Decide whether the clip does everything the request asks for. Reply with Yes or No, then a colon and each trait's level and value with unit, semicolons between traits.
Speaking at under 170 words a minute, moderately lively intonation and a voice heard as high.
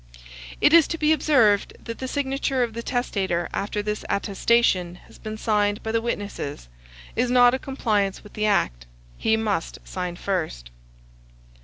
Yes: average, 160 wpm; average, 3.9 semitones; high, 215 Hz